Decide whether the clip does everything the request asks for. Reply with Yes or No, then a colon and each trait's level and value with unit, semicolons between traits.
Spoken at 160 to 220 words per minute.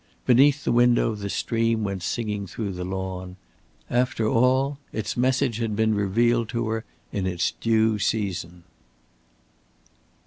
No: slow, 135 wpm